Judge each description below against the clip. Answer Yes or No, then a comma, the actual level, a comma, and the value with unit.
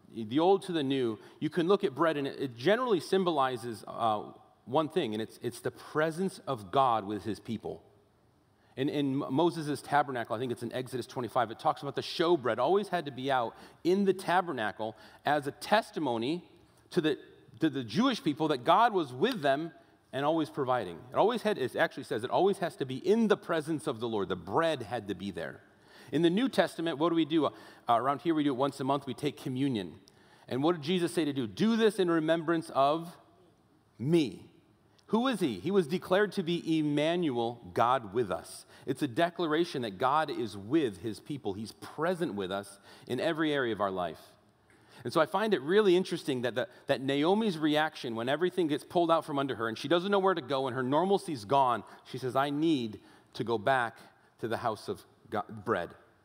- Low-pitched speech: No, medium, 150 Hz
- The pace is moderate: No, fast, 210 wpm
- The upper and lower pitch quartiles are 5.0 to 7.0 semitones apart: Yes, wide, 5.4 semitones